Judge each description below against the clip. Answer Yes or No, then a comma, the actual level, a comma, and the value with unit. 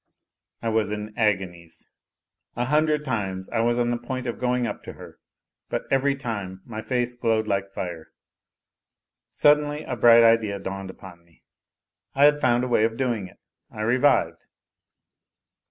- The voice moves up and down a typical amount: Yes, average, 4.2 semitones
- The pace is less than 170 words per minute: Yes, average, 160 wpm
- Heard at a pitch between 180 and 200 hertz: No, low, 115 Hz